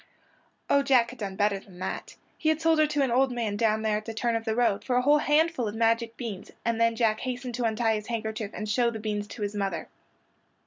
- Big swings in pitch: No, average, 2.7 semitones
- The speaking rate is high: Yes, fast, 255 wpm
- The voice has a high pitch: Yes, high, 230 Hz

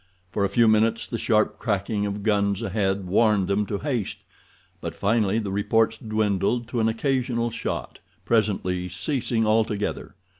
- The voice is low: Yes, low, 110 Hz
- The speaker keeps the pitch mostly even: Yes, narrow, 2.3 semitones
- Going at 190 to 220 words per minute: No, average, 150 wpm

